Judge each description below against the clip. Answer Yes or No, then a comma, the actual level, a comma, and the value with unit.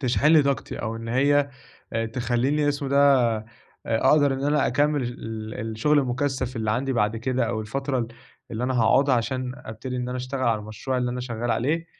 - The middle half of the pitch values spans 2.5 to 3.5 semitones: Yes, average, 3.1 semitones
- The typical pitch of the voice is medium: No, low, 130 Hz